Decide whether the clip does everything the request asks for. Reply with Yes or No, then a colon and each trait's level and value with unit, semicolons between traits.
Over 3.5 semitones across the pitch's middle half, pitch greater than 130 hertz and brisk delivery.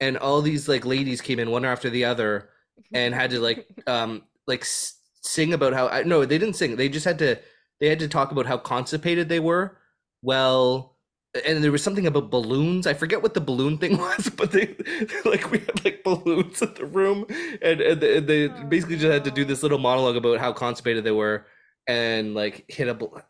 Yes: average, 5.1 semitones; medium, 140 Hz; fast, 210 wpm